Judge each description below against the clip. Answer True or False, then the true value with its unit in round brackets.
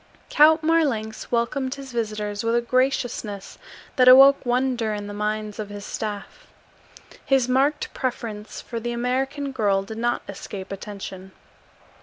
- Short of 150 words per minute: True (140 wpm)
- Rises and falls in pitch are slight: False (4.0 semitones)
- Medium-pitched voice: False (235 Hz)